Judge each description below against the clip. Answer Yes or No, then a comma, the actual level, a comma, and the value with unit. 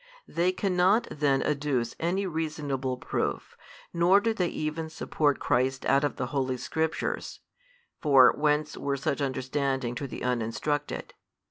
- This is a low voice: No, medium, 145 Hz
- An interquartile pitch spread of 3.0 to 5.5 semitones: Yes, average, 3.3 semitones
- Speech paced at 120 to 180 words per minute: Yes, average, 140 wpm